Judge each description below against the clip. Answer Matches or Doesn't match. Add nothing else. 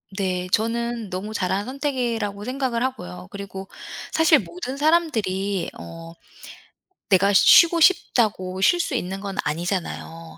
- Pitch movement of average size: Doesn't match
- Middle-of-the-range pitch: Doesn't match